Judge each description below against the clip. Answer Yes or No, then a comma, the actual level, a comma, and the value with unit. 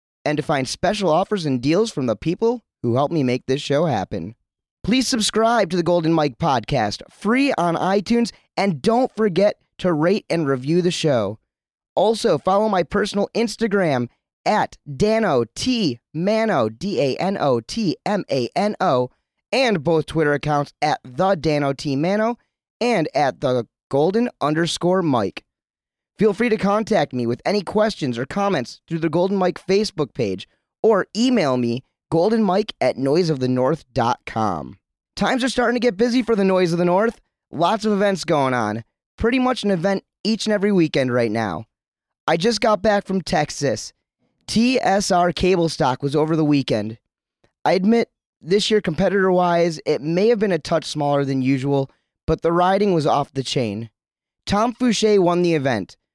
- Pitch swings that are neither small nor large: No, wide, 7.1 semitones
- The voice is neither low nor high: Yes, medium, 175 Hz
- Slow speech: No, average, 170 wpm